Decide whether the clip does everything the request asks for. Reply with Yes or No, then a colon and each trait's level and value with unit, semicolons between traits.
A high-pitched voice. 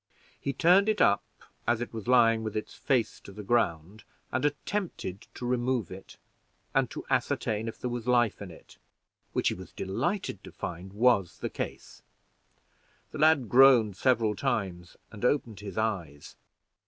No: low, 115 Hz